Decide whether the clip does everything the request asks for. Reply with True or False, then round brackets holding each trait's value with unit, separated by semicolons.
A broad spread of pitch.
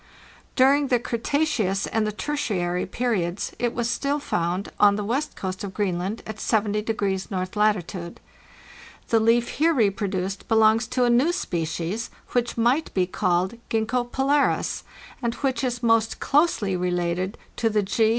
False (4.3 semitones)